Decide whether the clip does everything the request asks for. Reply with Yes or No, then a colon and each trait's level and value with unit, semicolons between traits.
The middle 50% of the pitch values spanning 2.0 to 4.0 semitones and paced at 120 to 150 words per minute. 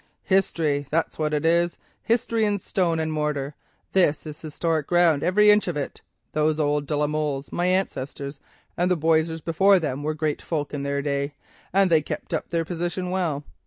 No: average, 3.2 semitones; average, 185 wpm